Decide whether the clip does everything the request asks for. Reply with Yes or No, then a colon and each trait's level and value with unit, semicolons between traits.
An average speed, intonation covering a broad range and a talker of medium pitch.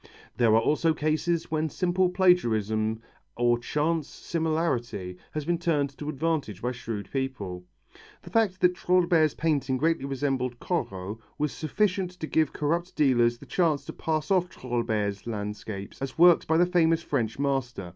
Yes: average, 155 wpm; wide, 5.9 semitones; medium, 145 Hz